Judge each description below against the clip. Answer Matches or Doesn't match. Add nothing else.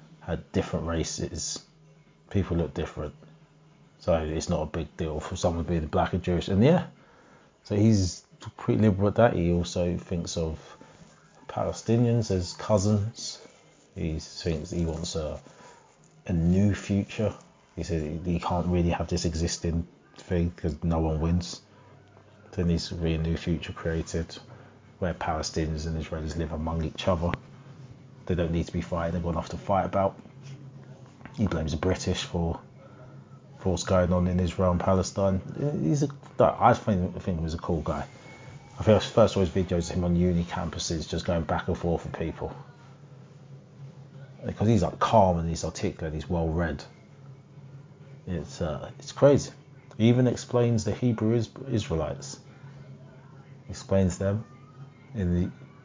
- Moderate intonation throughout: Doesn't match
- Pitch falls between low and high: Doesn't match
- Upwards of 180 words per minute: Doesn't match